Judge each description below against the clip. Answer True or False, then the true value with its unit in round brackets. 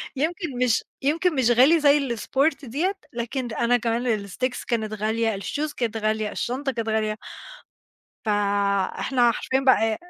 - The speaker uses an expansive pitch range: False (3.7 semitones)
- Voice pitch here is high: True (235 Hz)